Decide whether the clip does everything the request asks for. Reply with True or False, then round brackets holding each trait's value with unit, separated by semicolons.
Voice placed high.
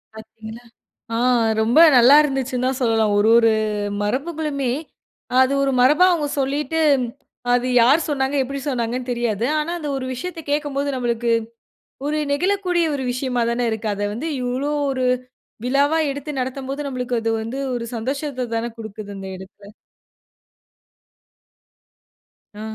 True (255 Hz)